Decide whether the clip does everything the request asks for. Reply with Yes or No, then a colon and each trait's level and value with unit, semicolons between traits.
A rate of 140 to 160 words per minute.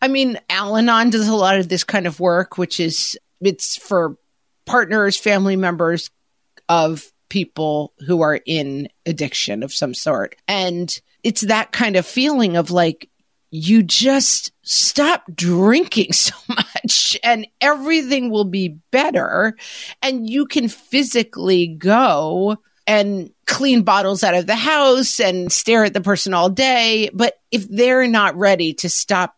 Yes: average, 145 wpm